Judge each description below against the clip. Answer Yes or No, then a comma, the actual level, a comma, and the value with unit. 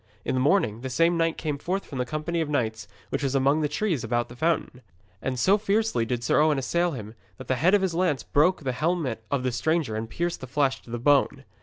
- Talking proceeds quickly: Yes, fast, 250 wpm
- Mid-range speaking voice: Yes, medium, 145 Hz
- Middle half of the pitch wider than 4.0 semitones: Yes, average, 5.2 semitones